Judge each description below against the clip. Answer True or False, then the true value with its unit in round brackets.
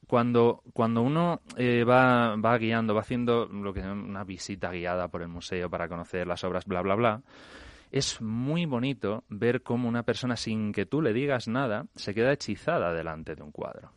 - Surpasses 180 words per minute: True (190 wpm)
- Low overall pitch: True (110 Hz)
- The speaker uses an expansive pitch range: False (4.7 semitones)